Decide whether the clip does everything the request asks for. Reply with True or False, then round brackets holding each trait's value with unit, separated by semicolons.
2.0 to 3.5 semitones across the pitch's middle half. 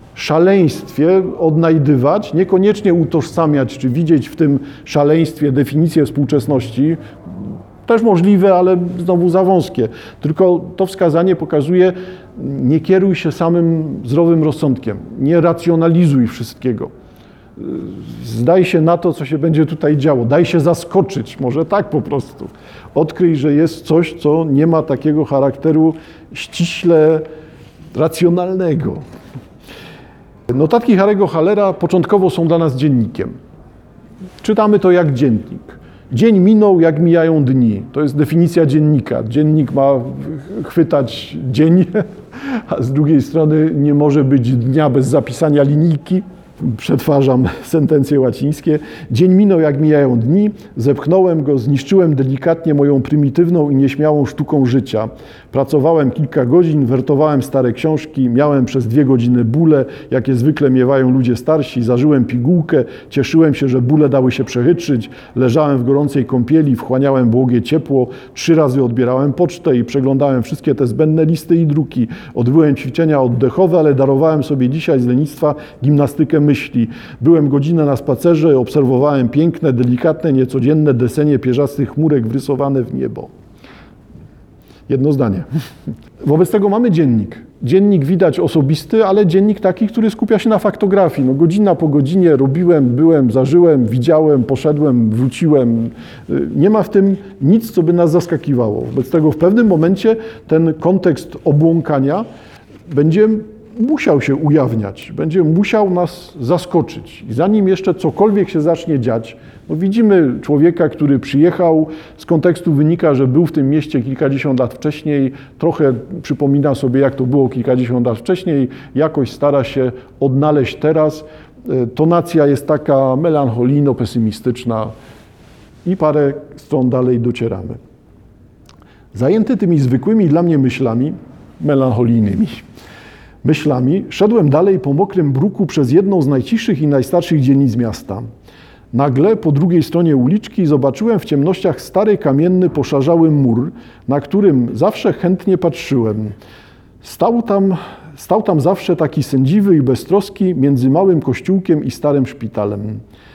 False (4.4 semitones)